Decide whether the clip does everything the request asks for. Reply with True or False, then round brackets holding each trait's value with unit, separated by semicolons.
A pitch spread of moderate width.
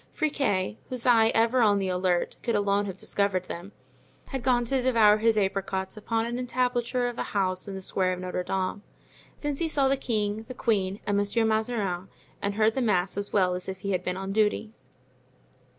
True (3.9 semitones)